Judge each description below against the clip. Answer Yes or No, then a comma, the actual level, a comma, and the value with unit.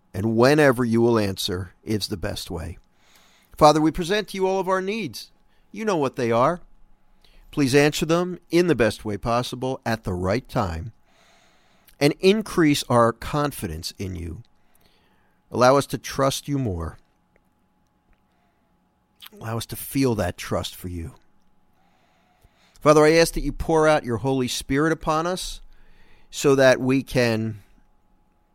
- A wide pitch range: Yes, wide, 6.2 semitones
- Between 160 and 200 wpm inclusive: No, average, 150 wpm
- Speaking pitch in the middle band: No, low, 125 Hz